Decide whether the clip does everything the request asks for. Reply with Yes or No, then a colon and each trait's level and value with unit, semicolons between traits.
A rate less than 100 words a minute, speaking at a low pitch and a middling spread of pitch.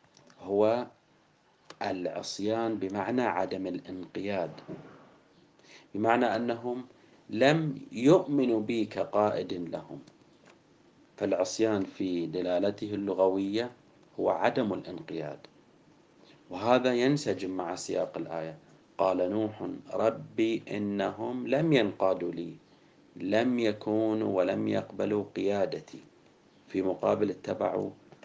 Yes: average, 85 wpm; low, 110 Hz; average, 3.9 semitones